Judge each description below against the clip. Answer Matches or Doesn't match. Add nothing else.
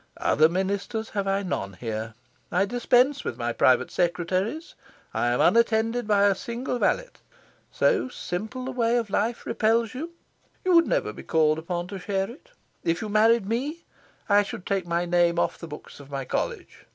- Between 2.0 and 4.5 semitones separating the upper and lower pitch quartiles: Doesn't match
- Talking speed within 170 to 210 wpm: Matches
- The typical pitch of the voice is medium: Doesn't match